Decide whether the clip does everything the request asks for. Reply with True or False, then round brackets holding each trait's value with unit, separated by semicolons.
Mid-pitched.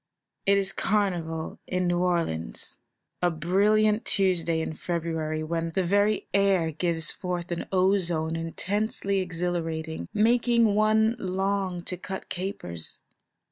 True (180 Hz)